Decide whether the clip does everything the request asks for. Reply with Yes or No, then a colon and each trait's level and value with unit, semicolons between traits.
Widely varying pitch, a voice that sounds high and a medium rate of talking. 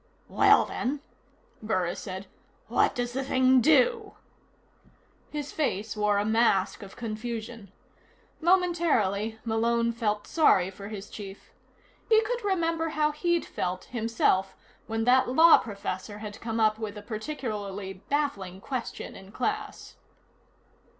No: wide, 6.2 semitones; high, 225 Hz; slow, 125 wpm